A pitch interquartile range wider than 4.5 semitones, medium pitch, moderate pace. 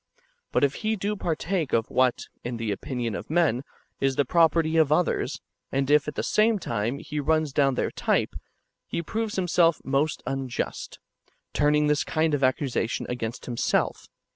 No: average, 4.1 semitones; medium, 145 Hz; average, 165 wpm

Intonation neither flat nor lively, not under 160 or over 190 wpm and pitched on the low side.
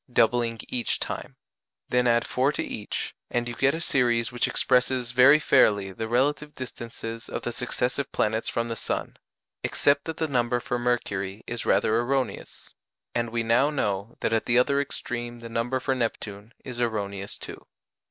No: narrow, 2.0 semitones; average, 170 wpm; low, 120 Hz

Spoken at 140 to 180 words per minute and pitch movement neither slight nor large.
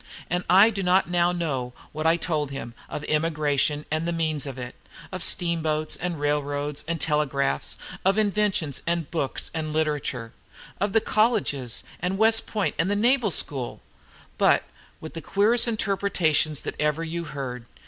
Yes: average, 160 wpm; average, 4.2 semitones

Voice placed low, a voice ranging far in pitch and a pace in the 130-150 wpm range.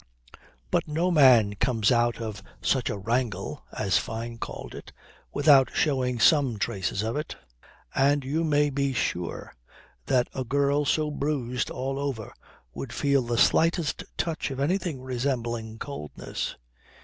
No: low, 130 Hz; average, 3.7 semitones; average, 140 wpm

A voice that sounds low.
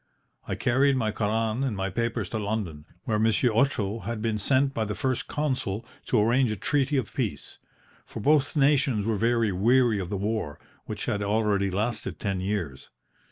Yes: low, 110 Hz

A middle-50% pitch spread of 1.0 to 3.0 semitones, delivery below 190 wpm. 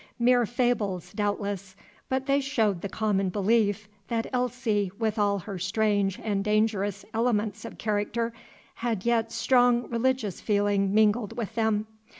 Yes: narrow, 2.6 semitones; average, 140 wpm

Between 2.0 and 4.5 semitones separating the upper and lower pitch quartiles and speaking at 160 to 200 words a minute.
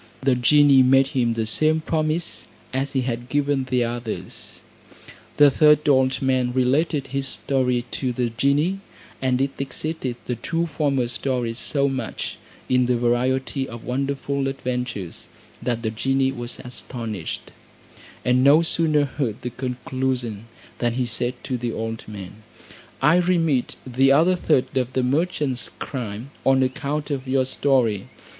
No: narrow, 2.4 semitones; average, 150 wpm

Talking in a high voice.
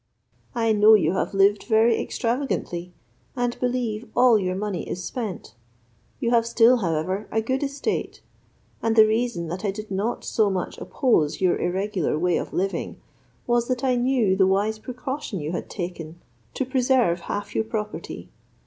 Yes: high, 215 Hz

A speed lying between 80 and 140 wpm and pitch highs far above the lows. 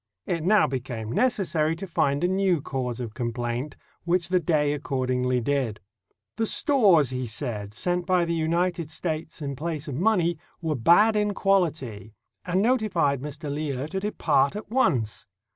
No: average, 160 wpm; wide, 6.0 semitones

